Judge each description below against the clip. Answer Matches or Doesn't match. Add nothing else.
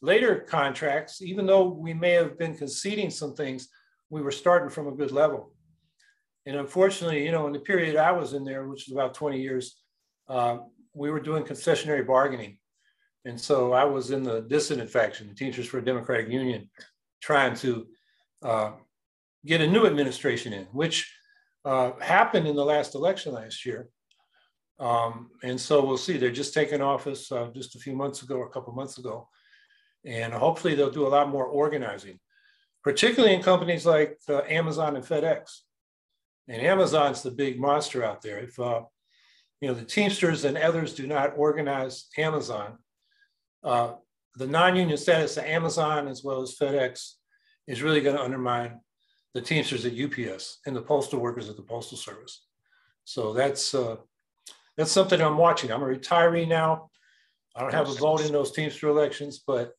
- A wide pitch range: Doesn't match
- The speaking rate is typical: Matches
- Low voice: Doesn't match